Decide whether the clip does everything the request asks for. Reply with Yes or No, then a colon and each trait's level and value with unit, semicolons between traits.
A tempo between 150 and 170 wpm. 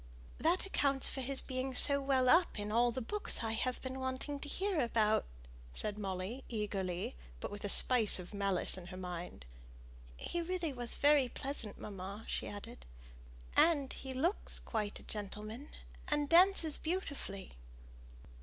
Yes: average, 155 wpm